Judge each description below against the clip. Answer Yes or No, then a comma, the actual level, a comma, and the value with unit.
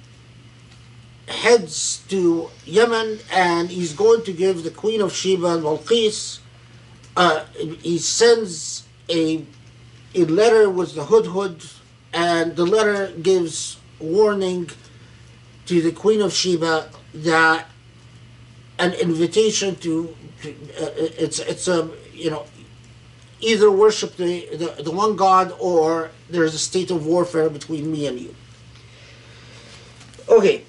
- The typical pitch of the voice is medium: Yes, medium, 160 Hz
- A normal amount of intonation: No, wide, 7.3 semitones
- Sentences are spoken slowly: Yes, slow, 120 wpm